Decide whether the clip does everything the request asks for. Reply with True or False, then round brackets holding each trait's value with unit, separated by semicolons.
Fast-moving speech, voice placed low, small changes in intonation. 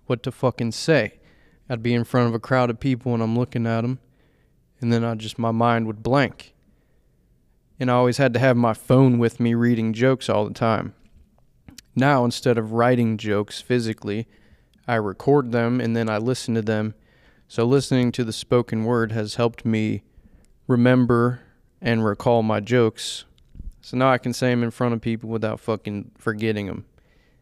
False (185 wpm; 115 Hz; 2.1 semitones)